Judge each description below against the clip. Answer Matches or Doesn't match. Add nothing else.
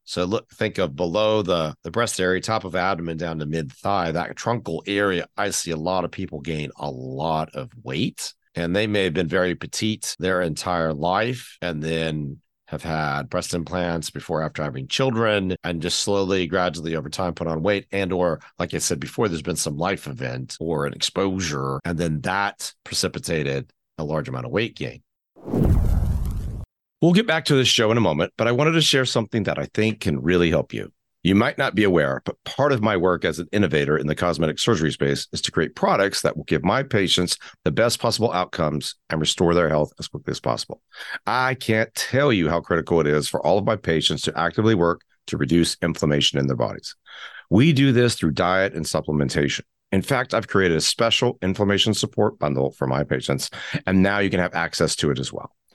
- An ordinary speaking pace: Doesn't match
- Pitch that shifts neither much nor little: Matches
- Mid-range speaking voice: Doesn't match